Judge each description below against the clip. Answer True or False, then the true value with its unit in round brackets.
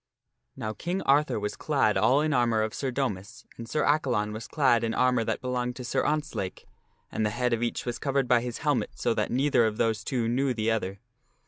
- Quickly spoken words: True (220 wpm)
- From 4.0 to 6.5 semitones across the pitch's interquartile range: False (3.5 semitones)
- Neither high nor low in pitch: False (120 Hz)